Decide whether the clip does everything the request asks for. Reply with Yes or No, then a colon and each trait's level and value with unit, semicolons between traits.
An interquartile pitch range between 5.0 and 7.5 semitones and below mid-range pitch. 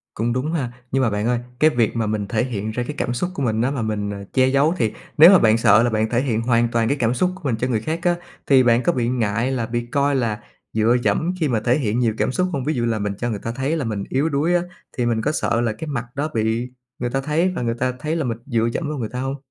No: average, 3.8 semitones; low, 120 Hz